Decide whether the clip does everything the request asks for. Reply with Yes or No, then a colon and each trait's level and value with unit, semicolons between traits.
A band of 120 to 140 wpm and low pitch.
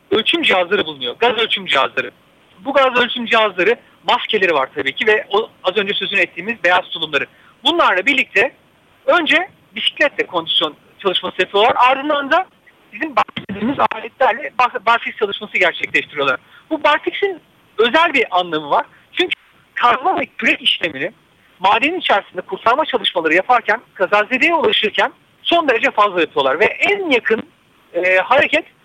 No: average, 130 wpm; high, 235 Hz